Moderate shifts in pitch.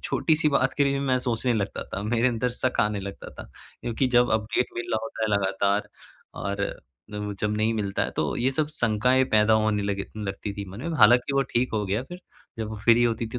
Yes: average, 3.2 semitones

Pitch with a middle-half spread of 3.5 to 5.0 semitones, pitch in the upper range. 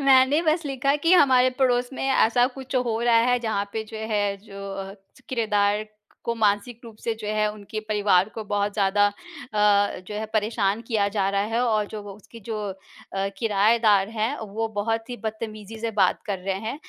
No: narrow, 2.5 semitones; high, 215 Hz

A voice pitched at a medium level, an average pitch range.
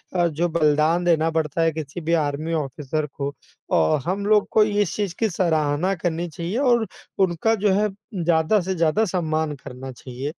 Yes: medium, 165 Hz; average, 3.8 semitones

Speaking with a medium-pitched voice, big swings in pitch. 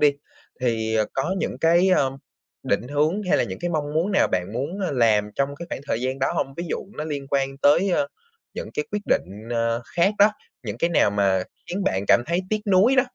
Yes: medium, 145 Hz; wide, 7.1 semitones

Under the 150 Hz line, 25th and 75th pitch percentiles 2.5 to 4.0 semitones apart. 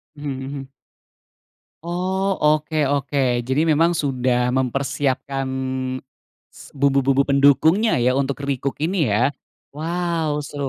Yes: medium, 140 Hz; average, 2.9 semitones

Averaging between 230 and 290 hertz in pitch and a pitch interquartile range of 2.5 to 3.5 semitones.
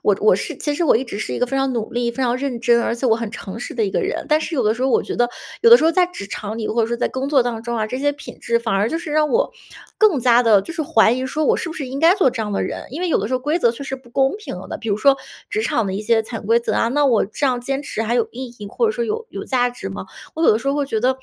No: very high, 250 Hz; average, 4.3 semitones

